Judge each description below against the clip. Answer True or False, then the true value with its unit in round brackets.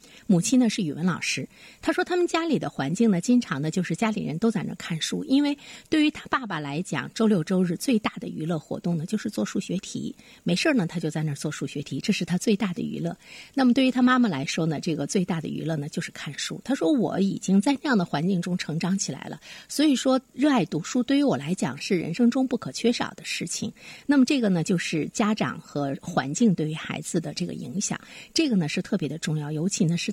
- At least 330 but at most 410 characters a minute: True (345 characters per minute)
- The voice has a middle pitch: False (200 Hz)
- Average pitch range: False (6.6 semitones)